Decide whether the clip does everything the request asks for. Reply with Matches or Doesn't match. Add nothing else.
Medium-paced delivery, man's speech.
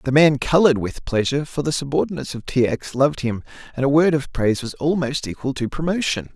Doesn't match